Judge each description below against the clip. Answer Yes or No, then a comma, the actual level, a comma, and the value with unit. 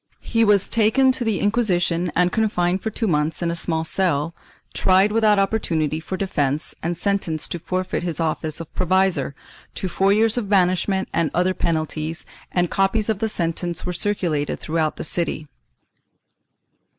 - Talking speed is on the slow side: No, average, 165 wpm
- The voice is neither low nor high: Yes, medium, 180 Hz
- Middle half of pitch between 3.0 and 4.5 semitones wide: Yes, average, 3.6 semitones